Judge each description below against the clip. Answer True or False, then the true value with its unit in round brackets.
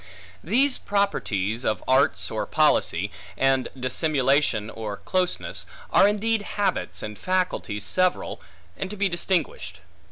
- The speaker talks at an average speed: False (120 wpm)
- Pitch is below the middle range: False (155 Hz)